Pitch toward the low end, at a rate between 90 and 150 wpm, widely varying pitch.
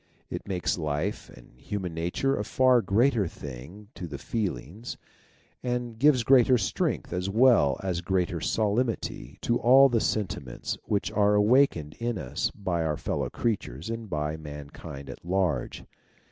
Yes: low, 100 Hz; average, 145 wpm; wide, 6.7 semitones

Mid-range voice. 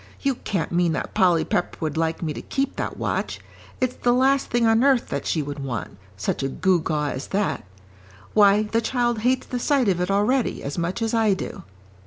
No: high, 200 Hz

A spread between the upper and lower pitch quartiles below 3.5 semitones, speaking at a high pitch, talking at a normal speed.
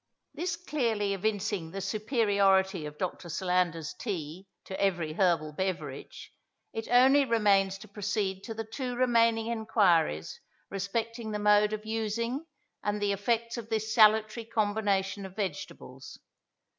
No: average, 2.9 semitones; high, 205 Hz; slow, 130 wpm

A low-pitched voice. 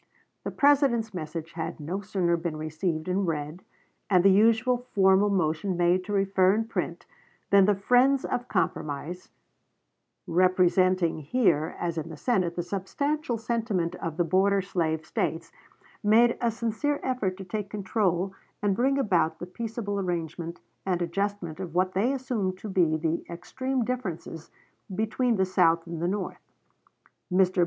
No: high, 190 Hz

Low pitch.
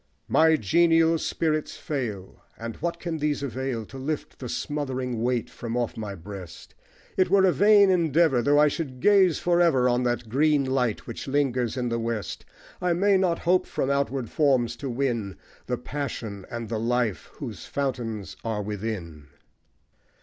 Yes: low, 130 Hz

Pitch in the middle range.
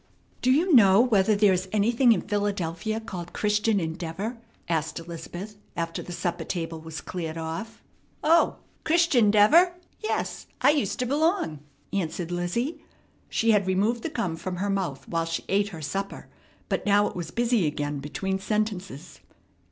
No: high, 195 Hz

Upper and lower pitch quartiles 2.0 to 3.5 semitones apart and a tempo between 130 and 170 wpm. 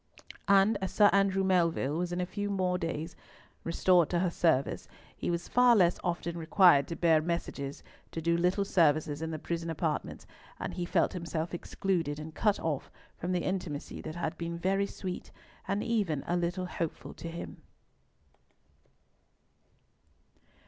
Yes: narrow, 2.4 semitones; average, 160 wpm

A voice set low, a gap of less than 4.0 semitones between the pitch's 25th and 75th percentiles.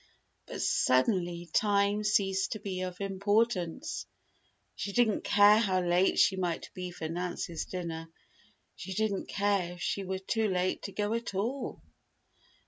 No: high, 195 Hz; narrow, 2.5 semitones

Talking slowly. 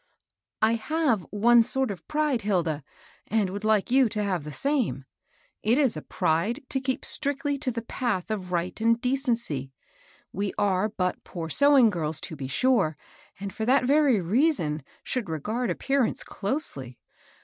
No: average, 170 wpm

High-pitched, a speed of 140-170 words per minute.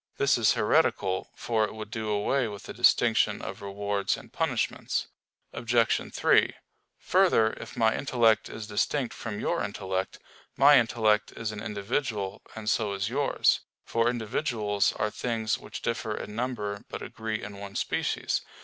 No: low, 110 Hz; average, 155 wpm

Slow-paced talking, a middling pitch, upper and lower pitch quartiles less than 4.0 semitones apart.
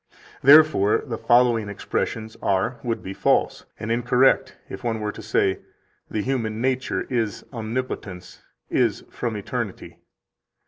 No: slow, 130 wpm; low, 115 Hz; average, 3.0 semitones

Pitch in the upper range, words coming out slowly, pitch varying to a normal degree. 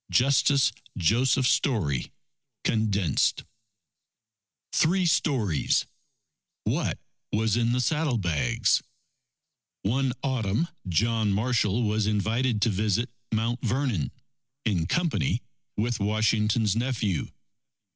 No: low, 110 Hz; slow, 85 wpm; average, 3.6 semitones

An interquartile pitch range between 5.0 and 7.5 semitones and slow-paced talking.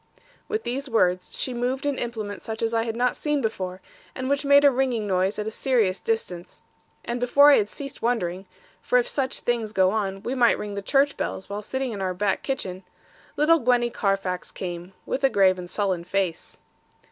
No: wide, 5.4 semitones; fast, 205 wpm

